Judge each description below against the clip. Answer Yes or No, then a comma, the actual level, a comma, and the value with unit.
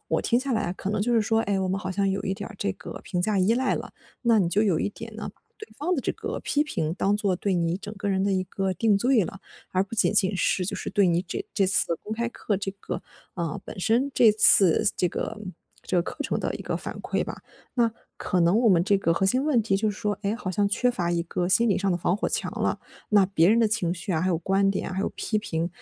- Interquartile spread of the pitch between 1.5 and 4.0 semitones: Yes, average, 3.1 semitones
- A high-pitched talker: Yes, high, 200 Hz